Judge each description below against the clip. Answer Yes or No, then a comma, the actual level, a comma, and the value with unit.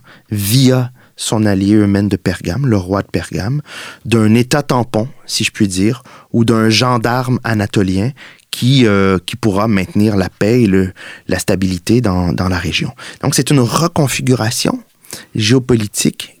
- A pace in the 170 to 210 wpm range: No, average, 150 wpm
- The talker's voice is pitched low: Yes, low, 110 Hz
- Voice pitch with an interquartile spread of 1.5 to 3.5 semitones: No, average, 4.1 semitones